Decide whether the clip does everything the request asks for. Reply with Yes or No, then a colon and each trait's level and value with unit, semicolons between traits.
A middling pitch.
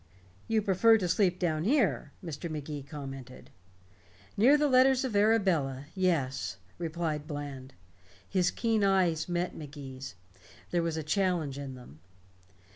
Yes: medium, 165 Hz